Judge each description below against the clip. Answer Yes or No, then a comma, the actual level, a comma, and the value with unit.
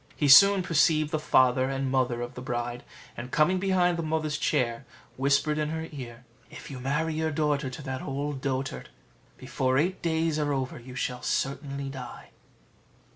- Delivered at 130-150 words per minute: No, average, 175 wpm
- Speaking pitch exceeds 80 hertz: Yes, medium, 140 Hz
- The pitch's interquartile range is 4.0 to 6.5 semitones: No, average, 3.3 semitones